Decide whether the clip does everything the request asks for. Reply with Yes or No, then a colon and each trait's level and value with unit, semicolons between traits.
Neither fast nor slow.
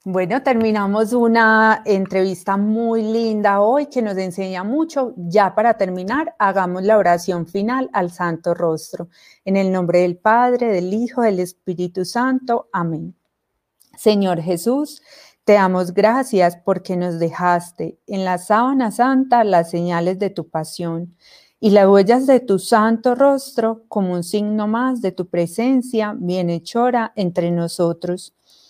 Yes: average, 140 wpm